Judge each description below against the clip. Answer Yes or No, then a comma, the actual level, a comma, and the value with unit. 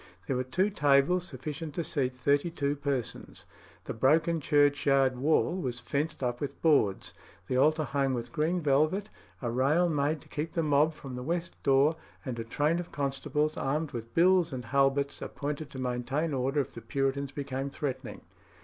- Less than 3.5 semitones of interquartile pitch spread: Yes, average, 2.9 semitones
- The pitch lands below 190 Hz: Yes, medium, 140 Hz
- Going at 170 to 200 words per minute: Yes, average, 175 wpm